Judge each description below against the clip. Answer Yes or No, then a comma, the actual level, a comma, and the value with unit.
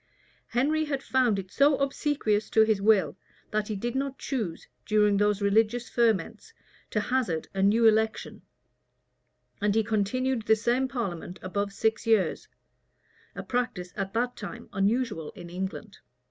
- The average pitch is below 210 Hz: No, high, 220 Hz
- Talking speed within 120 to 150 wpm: Yes, average, 145 wpm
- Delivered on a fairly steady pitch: No, average, 3.7 semitones